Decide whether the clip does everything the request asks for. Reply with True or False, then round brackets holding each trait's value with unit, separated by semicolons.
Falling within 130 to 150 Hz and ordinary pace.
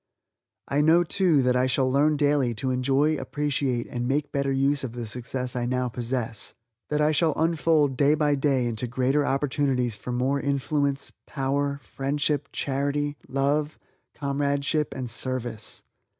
True (140 Hz; 150 wpm)